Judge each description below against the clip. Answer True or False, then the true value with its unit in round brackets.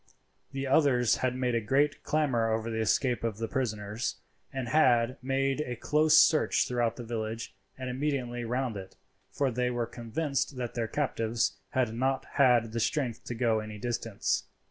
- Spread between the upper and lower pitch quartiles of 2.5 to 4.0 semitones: True (2.9 semitones)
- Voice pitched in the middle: False (125 Hz)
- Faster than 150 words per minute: True (170 wpm)